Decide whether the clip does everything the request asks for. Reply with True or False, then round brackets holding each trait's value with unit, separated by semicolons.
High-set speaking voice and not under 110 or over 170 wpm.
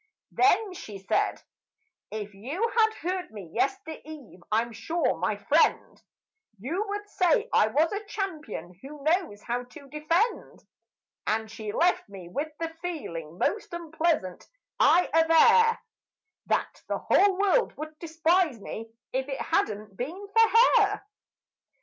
True (315 Hz; 135 wpm)